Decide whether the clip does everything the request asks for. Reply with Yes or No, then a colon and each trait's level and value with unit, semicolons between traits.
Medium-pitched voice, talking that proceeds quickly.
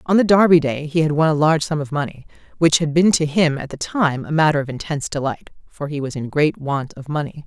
Yes: medium, 150 Hz; fast, 255 wpm